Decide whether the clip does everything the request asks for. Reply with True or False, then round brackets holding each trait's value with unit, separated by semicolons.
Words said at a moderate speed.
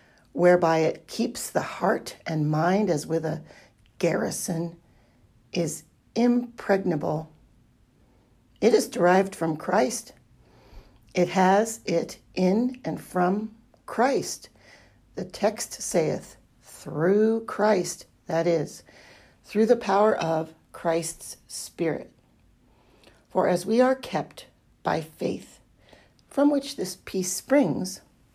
False (105 wpm)